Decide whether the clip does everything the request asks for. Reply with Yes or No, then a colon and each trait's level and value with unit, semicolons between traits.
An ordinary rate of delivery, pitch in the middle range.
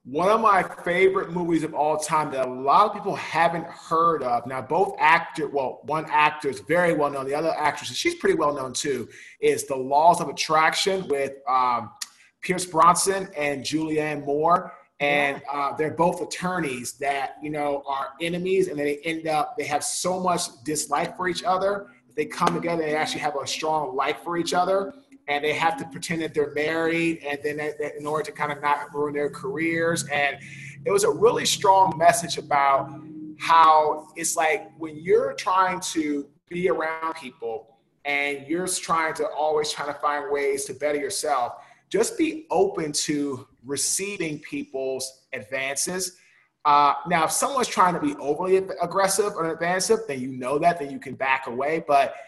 Yes: average, 180 wpm; medium, 155 Hz